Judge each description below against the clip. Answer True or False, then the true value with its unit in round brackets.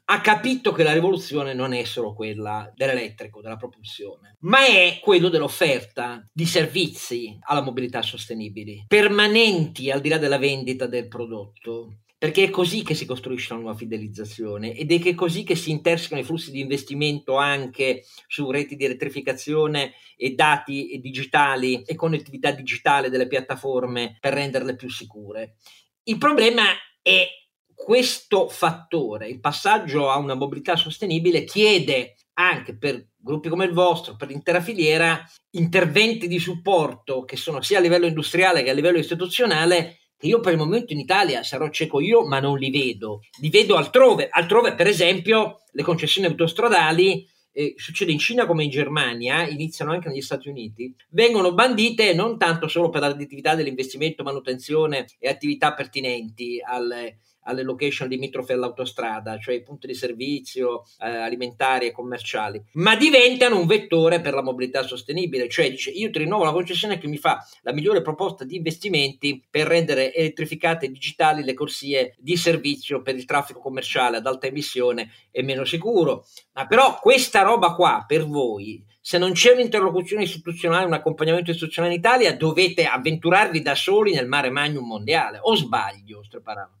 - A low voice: False (145 Hz)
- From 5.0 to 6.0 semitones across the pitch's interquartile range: True (5.3 semitones)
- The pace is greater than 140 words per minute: True (160 wpm)